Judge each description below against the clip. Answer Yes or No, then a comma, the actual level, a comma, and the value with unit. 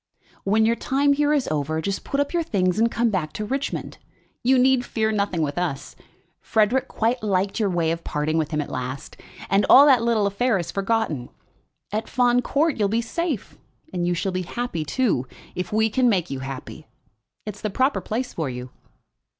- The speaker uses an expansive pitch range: Yes, wide, 6.3 semitones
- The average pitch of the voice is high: Yes, high, 210 Hz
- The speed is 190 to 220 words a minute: Yes, average, 200 wpm